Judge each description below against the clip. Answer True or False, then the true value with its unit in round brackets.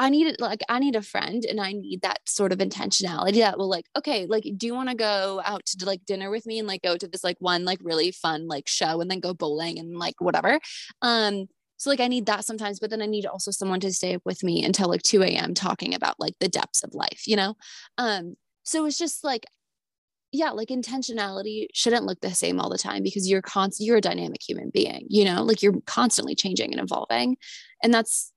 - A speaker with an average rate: False (240 wpm)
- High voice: True (200 Hz)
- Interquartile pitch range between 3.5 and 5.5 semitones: True (3.8 semitones)